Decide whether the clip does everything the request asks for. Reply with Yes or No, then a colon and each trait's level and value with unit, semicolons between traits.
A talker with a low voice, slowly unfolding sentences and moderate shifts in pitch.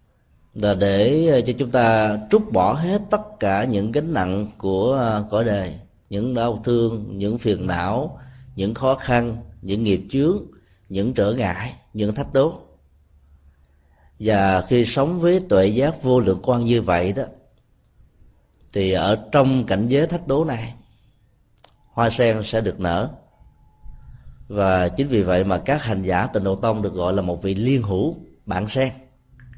Yes: low, 110 Hz; slow, 160 wpm; average, 4.8 semitones